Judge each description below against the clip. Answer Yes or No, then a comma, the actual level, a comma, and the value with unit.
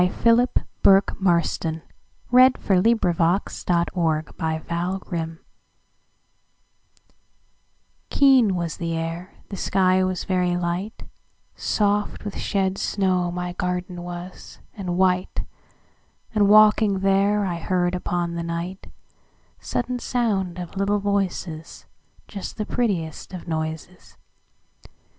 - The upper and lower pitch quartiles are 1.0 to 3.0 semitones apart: Yes, average, 2.7 semitones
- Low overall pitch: No, medium, 185 Hz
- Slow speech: Yes, slow, 90 wpm